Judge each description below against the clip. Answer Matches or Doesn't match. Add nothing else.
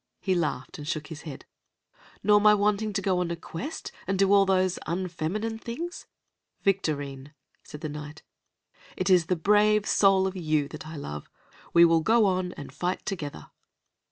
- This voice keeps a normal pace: Matches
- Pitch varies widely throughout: Doesn't match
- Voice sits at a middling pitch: Matches